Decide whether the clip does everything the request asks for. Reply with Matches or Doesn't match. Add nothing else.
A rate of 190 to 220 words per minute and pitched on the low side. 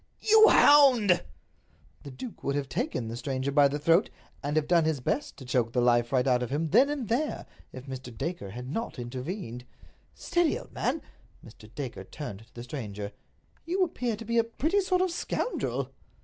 Doesn't match